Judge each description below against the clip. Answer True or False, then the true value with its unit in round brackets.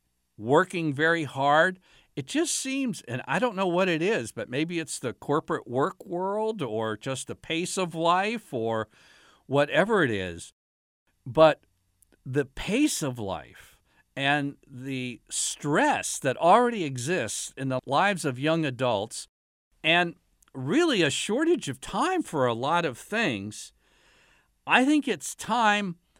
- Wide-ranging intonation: True (7.7 semitones)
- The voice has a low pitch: False (145 Hz)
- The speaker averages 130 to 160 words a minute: True (140 wpm)